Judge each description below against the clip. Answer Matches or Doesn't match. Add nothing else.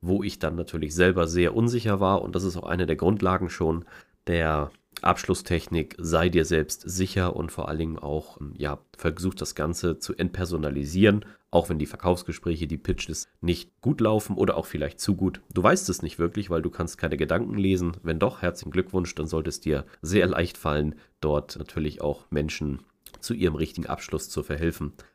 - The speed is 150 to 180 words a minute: Doesn't match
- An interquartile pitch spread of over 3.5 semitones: Doesn't match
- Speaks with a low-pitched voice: Matches